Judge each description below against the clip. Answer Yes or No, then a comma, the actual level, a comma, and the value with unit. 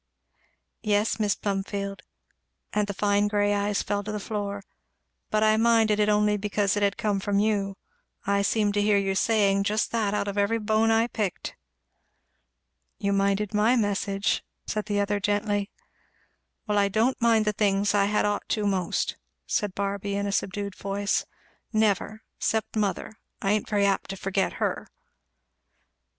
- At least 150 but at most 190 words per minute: Yes, average, 165 wpm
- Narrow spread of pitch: Yes, narrow, 1.1 semitones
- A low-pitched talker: No, high, 205 Hz